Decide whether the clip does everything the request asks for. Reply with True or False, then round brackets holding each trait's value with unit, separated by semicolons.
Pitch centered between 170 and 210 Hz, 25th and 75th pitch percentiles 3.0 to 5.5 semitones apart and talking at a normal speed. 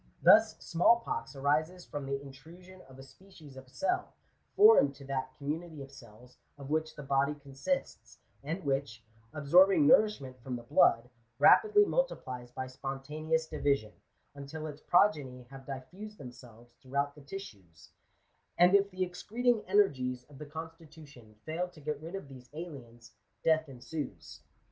False (145 Hz; 5.0 semitones; 150 wpm)